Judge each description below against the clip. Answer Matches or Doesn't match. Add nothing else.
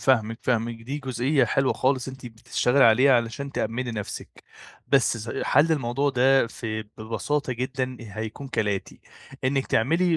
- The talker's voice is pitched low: Matches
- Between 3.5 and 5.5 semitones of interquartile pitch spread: Doesn't match